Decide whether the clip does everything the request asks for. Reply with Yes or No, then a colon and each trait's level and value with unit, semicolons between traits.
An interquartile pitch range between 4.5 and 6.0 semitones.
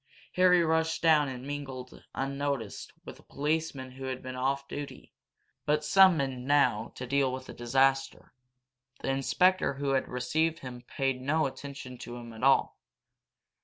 No: narrow, 2.5 semitones